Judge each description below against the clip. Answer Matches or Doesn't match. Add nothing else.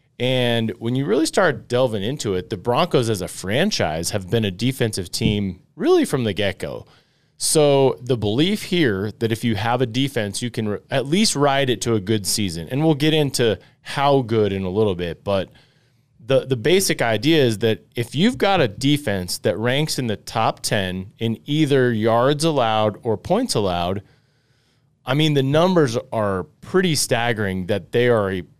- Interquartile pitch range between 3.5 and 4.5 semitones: Doesn't match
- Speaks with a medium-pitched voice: Doesn't match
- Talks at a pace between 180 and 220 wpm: Matches